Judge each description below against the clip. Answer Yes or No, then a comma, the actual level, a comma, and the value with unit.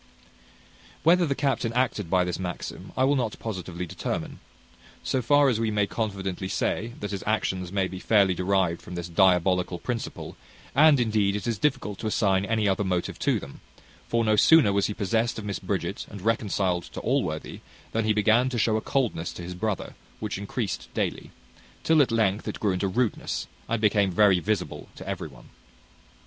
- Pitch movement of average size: Yes, average, 3.5 semitones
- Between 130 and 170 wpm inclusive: No, average, 185 wpm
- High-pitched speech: No, low, 105 Hz